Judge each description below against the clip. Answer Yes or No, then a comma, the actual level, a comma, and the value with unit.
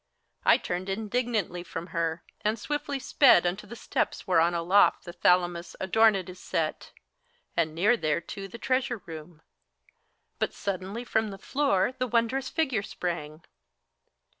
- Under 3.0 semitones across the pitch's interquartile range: No, average, 5.1 semitones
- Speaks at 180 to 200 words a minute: No, average, 140 wpm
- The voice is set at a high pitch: Yes, high, 195 Hz